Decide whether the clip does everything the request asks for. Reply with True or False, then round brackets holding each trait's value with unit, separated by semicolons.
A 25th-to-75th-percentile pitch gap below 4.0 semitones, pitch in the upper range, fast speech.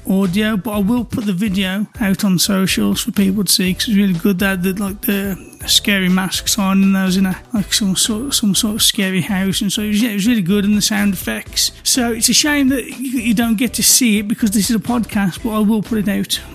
True (2.7 semitones; 205 Hz; 270 wpm)